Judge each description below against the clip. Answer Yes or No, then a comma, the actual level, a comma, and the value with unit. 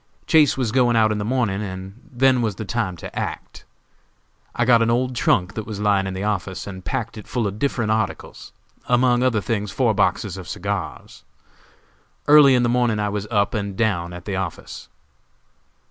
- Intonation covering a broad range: No, average, 3.5 semitones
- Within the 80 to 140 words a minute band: No, average, 190 wpm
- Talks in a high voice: No, low, 110 Hz